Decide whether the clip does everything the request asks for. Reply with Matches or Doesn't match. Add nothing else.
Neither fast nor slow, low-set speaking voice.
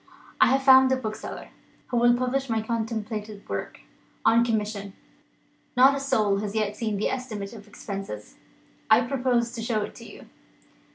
Doesn't match